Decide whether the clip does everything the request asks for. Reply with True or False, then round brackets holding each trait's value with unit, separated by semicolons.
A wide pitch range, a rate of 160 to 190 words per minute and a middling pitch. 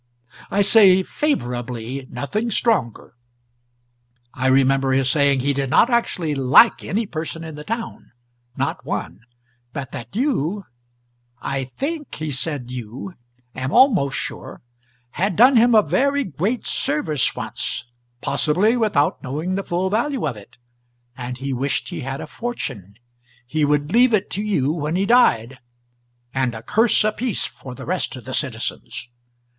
False (8.3 semitones; 150 wpm; 155 Hz)